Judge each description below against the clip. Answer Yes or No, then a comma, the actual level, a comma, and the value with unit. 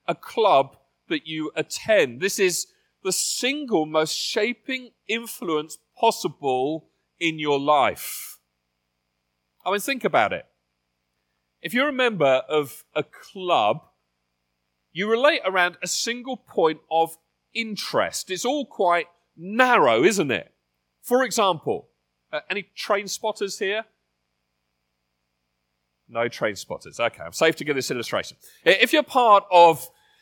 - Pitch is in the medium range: Yes, medium, 160 Hz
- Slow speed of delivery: Yes, slow, 125 wpm